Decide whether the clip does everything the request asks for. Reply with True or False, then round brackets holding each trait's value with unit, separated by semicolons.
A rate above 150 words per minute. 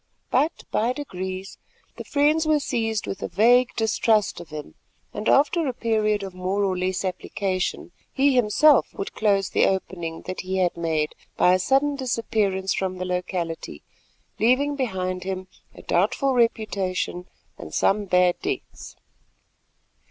False (145 wpm)